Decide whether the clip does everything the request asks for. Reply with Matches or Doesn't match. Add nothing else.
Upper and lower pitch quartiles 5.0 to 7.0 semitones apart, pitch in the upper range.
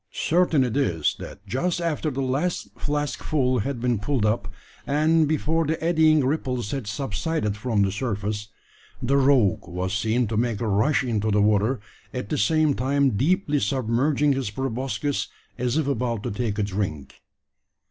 Doesn't match